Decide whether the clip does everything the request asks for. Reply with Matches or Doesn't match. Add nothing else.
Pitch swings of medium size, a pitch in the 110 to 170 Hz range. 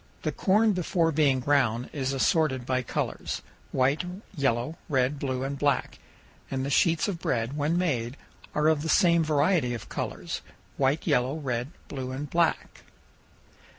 Matches